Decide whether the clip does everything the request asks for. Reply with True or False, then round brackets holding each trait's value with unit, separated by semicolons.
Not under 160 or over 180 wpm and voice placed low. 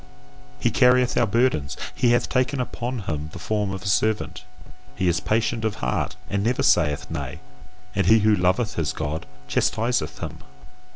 True (170 wpm; 105 Hz)